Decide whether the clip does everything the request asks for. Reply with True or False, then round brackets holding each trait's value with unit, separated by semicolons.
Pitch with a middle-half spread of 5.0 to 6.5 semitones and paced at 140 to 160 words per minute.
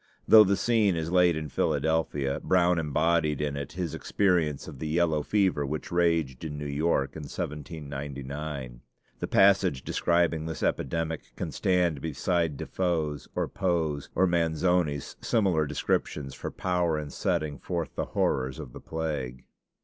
False (3.2 semitones; 150 wpm)